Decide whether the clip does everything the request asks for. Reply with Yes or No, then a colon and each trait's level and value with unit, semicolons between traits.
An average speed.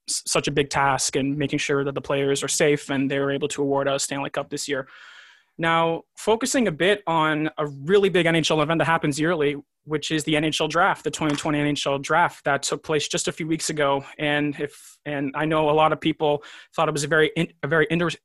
No: fast, 230 wpm